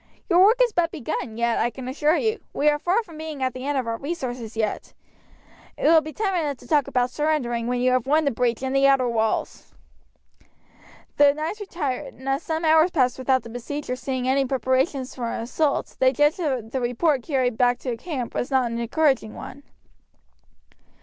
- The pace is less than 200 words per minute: No, fast, 205 wpm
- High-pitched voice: Yes, very high, 265 Hz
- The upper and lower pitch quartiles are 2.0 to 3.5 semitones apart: No, average, 4.0 semitones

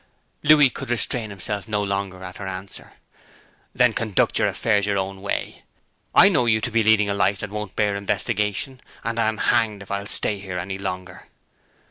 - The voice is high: No, low, 105 Hz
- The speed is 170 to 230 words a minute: Yes, average, 185 wpm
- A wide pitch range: No, narrow, 2.5 semitones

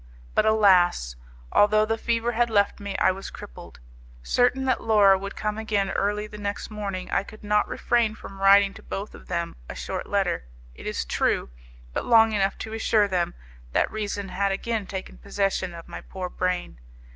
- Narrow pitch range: Yes, narrow, 2.1 semitones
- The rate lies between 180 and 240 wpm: Yes, average, 185 wpm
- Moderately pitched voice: No, high, 200 Hz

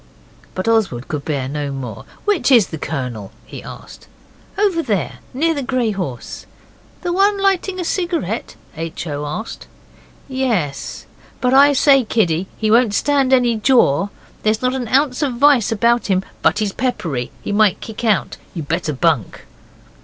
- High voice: Yes, high, 220 Hz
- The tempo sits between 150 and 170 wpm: Yes, average, 160 wpm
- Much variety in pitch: Yes, wide, 8.6 semitones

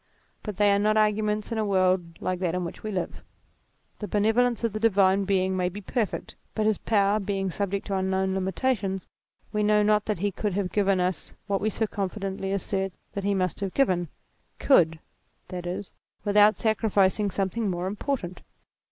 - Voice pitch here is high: Yes, high, 200 Hz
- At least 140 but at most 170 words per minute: No, average, 185 wpm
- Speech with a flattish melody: Yes, narrow, 2.0 semitones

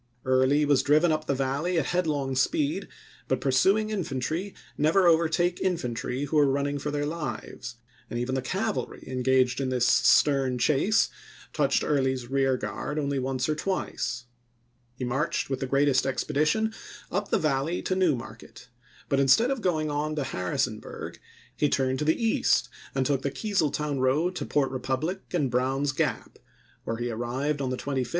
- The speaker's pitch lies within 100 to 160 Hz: Yes, medium, 140 Hz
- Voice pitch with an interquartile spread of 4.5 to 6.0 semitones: No, average, 3.5 semitones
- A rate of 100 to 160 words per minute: No, average, 170 wpm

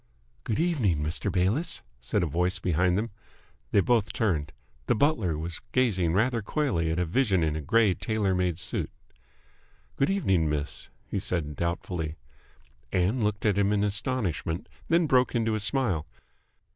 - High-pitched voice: No, very low, 95 Hz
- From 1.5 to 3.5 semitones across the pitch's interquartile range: No, average, 5.3 semitones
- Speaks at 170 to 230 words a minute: No, average, 160 wpm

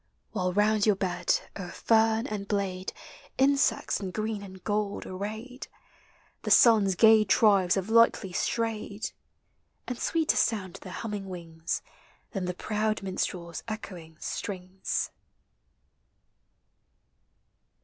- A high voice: Yes, high, 205 Hz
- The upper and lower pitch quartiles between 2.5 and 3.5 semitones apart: Yes, average, 2.9 semitones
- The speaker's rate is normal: No, slow, 110 wpm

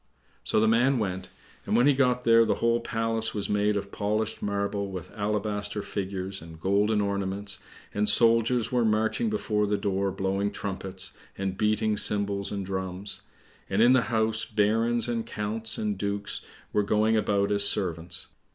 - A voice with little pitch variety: Yes, narrow, 2.1 semitones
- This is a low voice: Yes, low, 105 Hz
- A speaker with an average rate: Yes, average, 165 wpm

